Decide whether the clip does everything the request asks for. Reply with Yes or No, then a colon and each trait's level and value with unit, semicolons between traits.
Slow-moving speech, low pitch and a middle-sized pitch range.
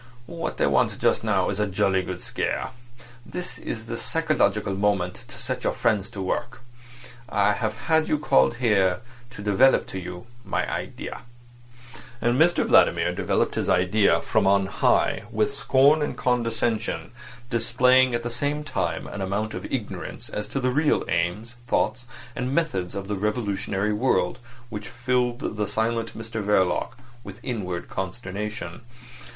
No: average, 155 wpm; low, 110 Hz; average, 4.0 semitones